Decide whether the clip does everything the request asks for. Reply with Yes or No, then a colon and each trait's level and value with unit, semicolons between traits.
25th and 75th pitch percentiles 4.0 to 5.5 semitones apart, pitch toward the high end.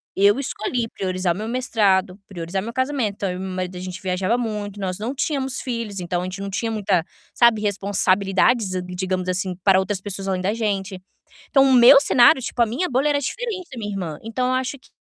Yes: average, 4.6 semitones; high, 205 Hz